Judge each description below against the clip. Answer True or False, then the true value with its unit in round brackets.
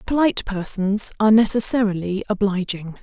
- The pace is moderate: False (100 wpm)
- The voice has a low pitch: False (205 Hz)